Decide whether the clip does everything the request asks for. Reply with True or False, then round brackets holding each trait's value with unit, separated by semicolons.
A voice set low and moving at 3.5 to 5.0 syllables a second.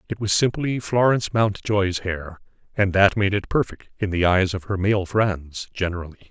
True (100 Hz; 4.8 syllables/s)